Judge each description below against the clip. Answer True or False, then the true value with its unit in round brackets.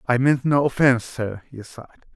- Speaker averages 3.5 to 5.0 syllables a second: False (5.8 syllables/s)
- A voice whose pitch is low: True (125 Hz)